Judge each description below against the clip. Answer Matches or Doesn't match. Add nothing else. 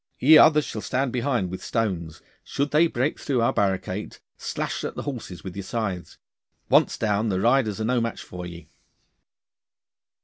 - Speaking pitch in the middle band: Doesn't match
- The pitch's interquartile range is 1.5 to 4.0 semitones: Doesn't match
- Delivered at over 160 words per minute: Matches